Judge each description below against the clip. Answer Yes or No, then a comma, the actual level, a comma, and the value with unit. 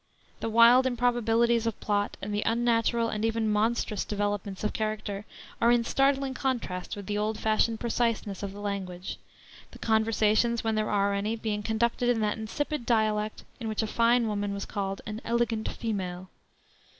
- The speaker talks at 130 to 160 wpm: No, average, 170 wpm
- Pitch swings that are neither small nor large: No, narrow, 2.1 semitones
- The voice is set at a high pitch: Yes, high, 220 Hz